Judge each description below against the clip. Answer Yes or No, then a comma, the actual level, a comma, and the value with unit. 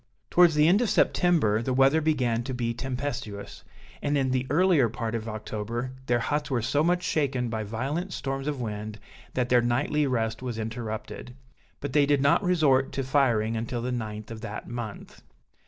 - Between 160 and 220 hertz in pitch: No, low, 125 Hz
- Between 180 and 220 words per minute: Yes, average, 185 wpm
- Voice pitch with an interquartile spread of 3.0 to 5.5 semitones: Yes, average, 4.1 semitones